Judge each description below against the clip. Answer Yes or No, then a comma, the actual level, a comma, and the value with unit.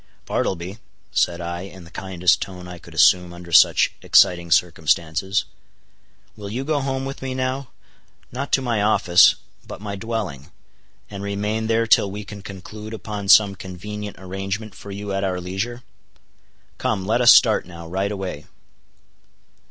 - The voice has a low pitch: Yes, low, 100 Hz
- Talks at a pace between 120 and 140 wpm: No, average, 150 wpm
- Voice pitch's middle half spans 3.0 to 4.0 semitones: Yes, average, 3.4 semitones